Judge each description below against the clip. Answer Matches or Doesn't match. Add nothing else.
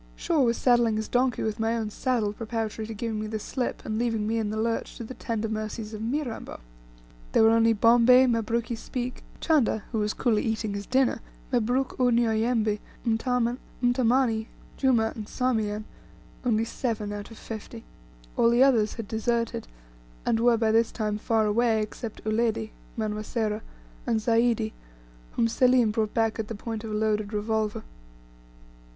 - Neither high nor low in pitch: Doesn't match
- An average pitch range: Doesn't match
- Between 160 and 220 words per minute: Matches